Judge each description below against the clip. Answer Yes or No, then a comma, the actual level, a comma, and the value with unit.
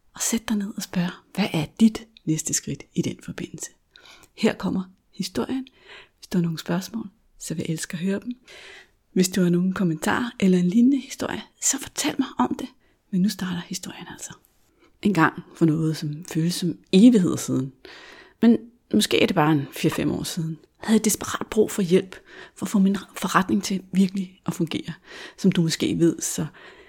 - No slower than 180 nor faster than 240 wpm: Yes, average, 195 wpm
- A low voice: No, high, 190 Hz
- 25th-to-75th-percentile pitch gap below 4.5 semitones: No, average, 4.8 semitones